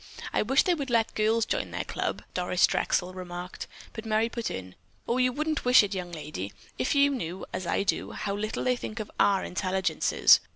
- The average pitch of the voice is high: Yes, high, 215 Hz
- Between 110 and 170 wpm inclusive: No, average, 200 wpm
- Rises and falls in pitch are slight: No, average, 5.1 semitones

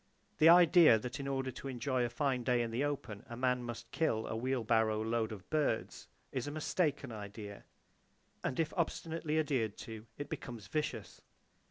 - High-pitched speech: No, low, 125 Hz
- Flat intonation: No, average, 4.4 semitones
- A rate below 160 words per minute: No, average, 180 wpm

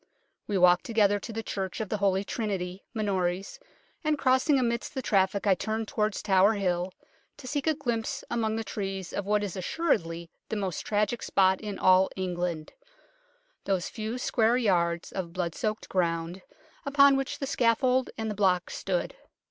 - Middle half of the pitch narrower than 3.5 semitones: No, average, 3.8 semitones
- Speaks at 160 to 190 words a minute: Yes, average, 170 wpm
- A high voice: Yes, high, 205 Hz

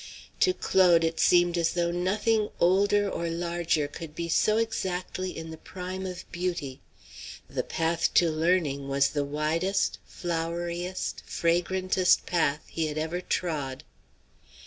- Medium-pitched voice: Yes, medium, 170 Hz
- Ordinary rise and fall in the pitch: No, narrow, 2.3 semitones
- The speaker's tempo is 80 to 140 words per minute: Yes, slow, 135 wpm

